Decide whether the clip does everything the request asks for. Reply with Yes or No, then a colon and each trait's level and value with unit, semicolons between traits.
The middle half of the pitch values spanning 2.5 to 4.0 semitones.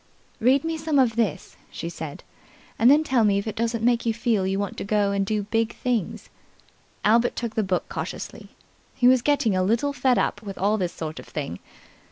Yes: average, 3.6 semitones